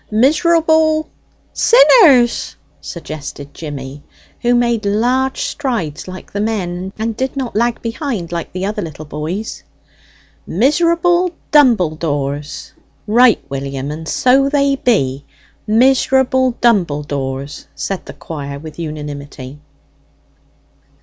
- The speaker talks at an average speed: No, slow, 105 wpm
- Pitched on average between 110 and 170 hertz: No, high, 210 Hz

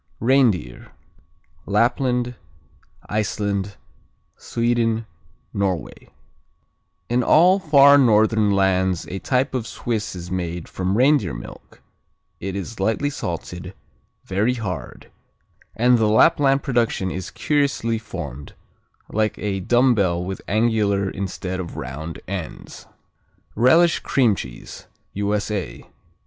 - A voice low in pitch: Yes, low, 105 Hz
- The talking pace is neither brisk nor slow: No, slow, 105 wpm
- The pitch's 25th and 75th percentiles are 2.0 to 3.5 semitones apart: No, average, 4.6 semitones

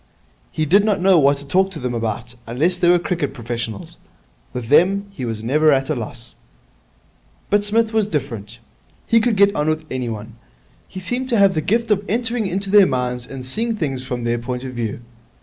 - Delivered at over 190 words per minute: Yes, average, 200 wpm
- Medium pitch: Yes, medium, 150 Hz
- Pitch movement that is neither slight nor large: No, wide, 8.3 semitones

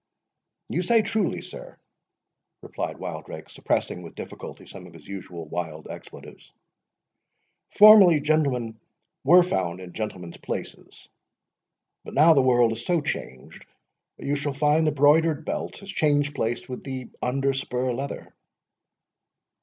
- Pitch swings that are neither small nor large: No, wide, 6.4 semitones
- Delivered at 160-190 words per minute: No, slow, 135 wpm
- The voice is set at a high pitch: No, low, 135 Hz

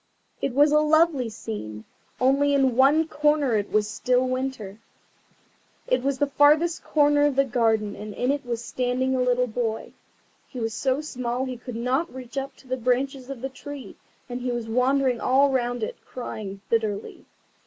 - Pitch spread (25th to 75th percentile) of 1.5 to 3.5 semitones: Yes, average, 2.9 semitones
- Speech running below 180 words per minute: No, average, 185 wpm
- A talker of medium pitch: No, very high, 255 Hz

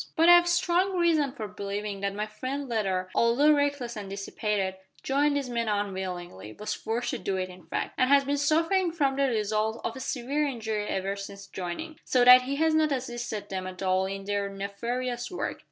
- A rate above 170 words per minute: Yes, average, 200 wpm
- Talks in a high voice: Yes, high, 230 Hz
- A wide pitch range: Yes, wide, 6.1 semitones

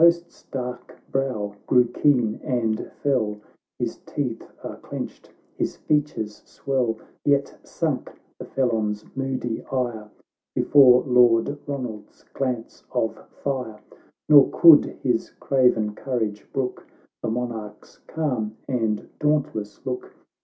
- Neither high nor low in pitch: No, low, 125 Hz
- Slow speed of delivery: Yes, slow, 115 wpm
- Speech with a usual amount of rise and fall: Yes, average, 3.6 semitones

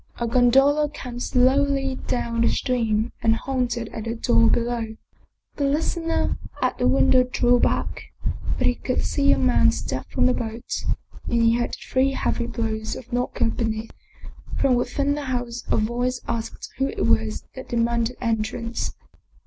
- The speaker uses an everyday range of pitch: No, narrow, 2.2 semitones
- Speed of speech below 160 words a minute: No, average, 165 wpm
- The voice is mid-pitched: No, high, 240 Hz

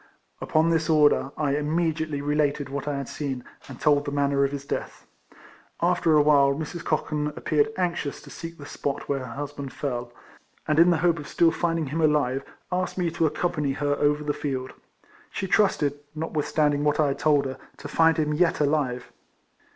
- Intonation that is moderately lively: No, narrow, 2.2 semitones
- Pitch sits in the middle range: Yes, medium, 150 Hz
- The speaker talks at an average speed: Yes, average, 185 wpm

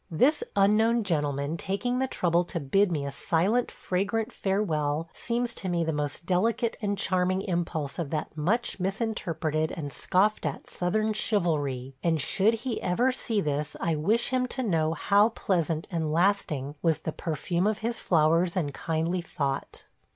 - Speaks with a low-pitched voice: No, medium, 180 Hz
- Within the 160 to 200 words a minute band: Yes, average, 165 wpm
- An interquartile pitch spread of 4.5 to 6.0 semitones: Yes, average, 5.3 semitones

